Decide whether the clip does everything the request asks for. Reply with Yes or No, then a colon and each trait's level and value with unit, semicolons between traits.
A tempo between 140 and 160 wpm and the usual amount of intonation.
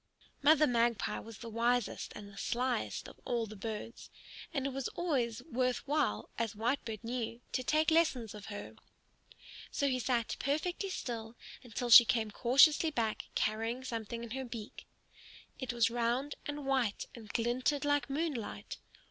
Yes: average, 155 wpm; average, 3.4 semitones